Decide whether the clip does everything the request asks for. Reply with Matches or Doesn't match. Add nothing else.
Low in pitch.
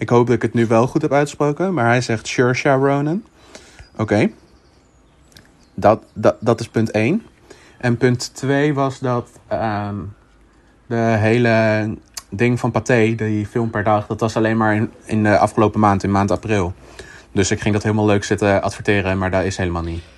Matches